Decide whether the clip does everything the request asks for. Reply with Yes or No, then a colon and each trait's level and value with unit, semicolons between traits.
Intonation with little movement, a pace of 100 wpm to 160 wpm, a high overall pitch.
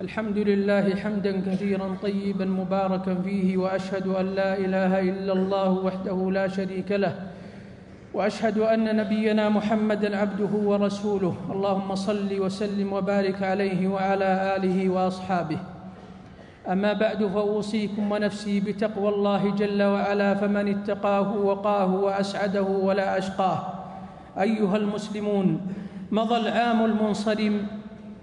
Yes: narrow, 1.5 semitones; average, 105 wpm; high, 200 Hz